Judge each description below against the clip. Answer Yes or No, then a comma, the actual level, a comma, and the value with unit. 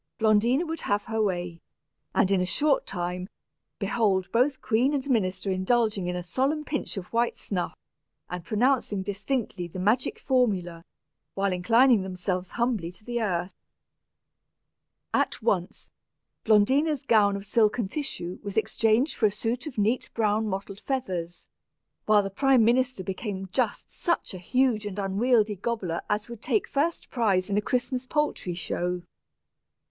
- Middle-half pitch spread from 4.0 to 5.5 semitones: Yes, average, 4.7 semitones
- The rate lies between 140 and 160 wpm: Yes, average, 150 wpm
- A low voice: No, high, 210 Hz